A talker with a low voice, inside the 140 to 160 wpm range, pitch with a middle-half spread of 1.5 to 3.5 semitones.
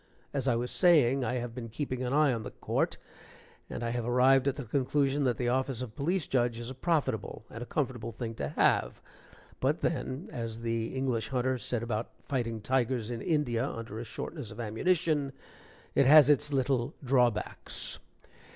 No: low, 125 Hz; average, 185 wpm; average, 2.9 semitones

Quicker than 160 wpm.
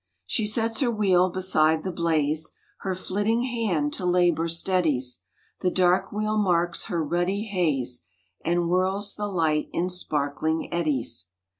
No: average, 140 wpm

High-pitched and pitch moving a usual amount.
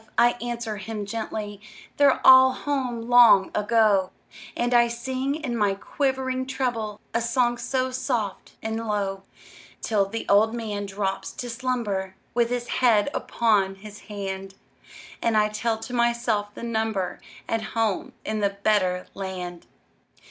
Yes: high, 225 Hz; average, 3.0 semitones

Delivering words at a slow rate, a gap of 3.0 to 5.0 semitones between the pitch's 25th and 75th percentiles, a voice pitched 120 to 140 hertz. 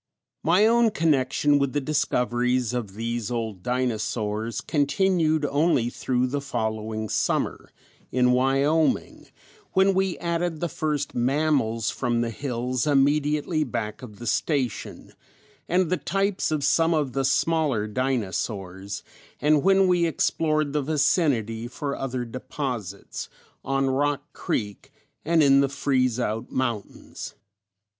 Yes: slow, 130 wpm; average, 4.5 semitones; low, 135 Hz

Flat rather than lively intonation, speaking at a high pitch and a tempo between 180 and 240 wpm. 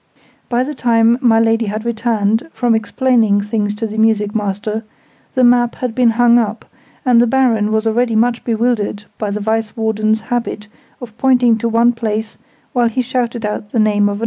Yes: narrow, 2.1 semitones; high, 225 Hz; average, 190 wpm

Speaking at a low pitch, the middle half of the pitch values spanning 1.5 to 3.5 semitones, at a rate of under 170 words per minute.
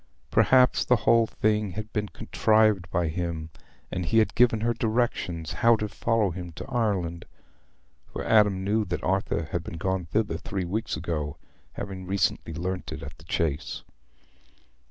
No: very low, 95 Hz; average, 4.3 semitones; average, 155 wpm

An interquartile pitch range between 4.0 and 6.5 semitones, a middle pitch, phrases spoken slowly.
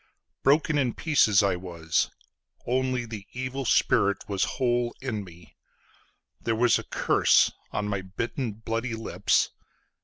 No: average, 4.5 semitones; low, 115 Hz; slow, 120 wpm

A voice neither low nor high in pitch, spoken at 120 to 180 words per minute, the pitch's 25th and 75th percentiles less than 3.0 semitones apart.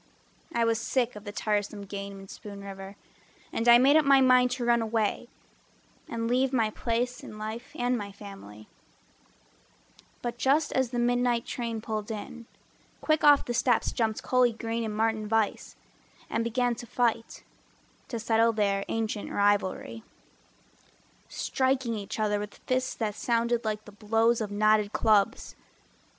No: high, 225 Hz; average, 155 wpm; narrow, 2.5 semitones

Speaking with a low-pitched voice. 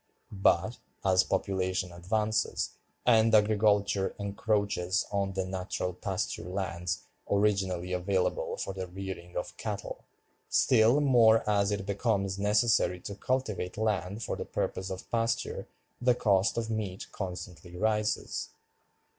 Yes: low, 100 Hz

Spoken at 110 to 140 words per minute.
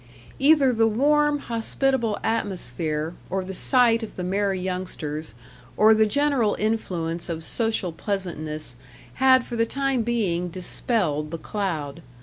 Yes: slow, 135 wpm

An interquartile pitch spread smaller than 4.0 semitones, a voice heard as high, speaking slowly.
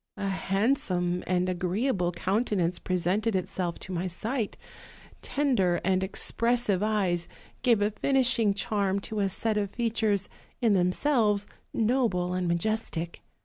Yes: average, 3.6 semitones; high, 200 Hz; slow, 130 wpm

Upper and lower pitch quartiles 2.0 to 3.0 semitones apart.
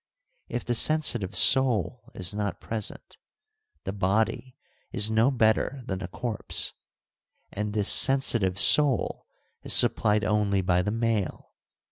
No: average, 3.4 semitones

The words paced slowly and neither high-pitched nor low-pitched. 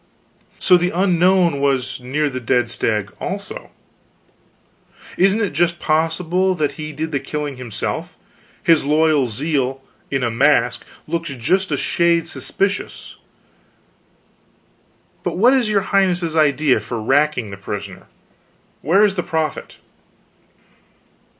Yes: slow, 125 wpm; medium, 155 Hz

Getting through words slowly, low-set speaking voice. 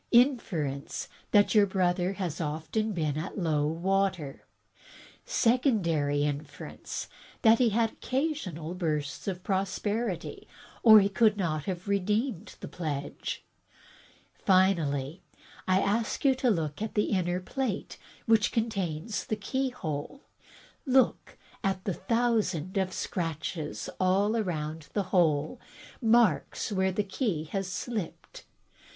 No: slow, 120 wpm; high, 190 Hz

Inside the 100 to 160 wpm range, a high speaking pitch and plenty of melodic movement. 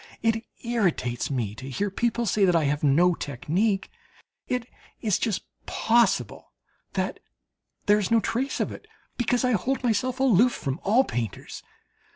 Yes: average, 155 wpm; high, 210 Hz; wide, 7.5 semitones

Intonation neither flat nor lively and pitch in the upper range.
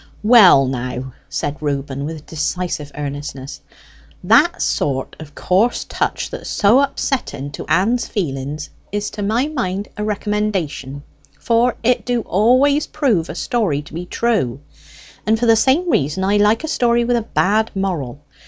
No: wide, 8.3 semitones; high, 195 Hz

